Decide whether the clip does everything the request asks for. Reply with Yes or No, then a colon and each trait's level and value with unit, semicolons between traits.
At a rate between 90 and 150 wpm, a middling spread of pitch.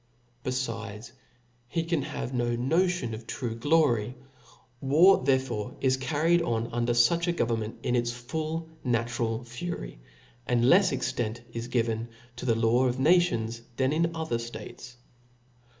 Yes: average, 145 wpm; average, 4.8 semitones